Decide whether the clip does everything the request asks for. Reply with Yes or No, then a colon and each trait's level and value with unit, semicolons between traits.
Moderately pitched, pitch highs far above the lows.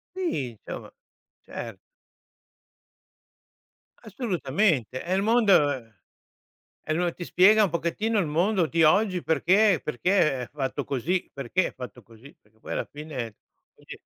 Yes: medium, 165 Hz; wide, 6.3 semitones